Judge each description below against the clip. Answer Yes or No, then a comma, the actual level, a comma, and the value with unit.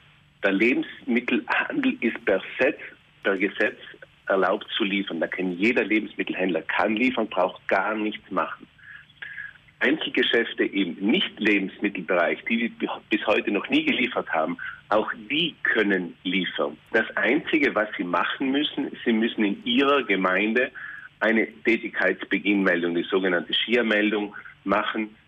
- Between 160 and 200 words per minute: No, slow, 125 wpm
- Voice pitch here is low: Yes, low, 110 Hz